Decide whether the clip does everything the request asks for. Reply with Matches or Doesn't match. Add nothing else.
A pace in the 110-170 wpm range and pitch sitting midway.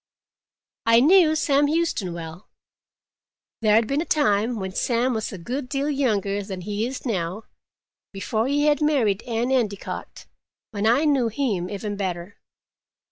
Doesn't match